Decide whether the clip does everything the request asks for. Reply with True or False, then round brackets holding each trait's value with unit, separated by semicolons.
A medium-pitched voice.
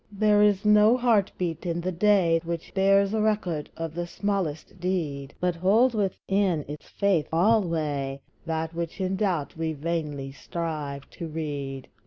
True (170 Hz)